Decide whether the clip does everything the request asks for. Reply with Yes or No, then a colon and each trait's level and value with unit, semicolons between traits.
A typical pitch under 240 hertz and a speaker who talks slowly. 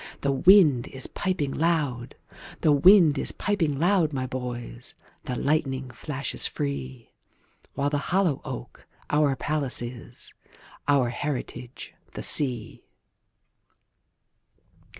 Yes: medium, 140 Hz; slow, 90 wpm